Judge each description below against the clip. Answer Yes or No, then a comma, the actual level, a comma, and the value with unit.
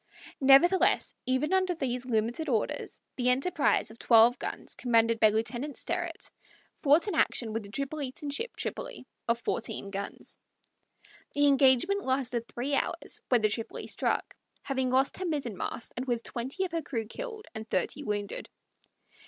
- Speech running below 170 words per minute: Yes, average, 155 wpm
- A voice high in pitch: Yes, very high, 260 Hz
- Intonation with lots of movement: No, average, 4.3 semitones